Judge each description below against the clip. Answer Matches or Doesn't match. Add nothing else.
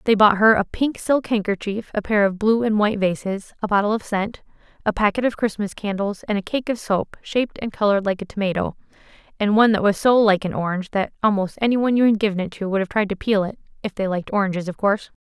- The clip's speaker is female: Matches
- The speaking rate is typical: Doesn't match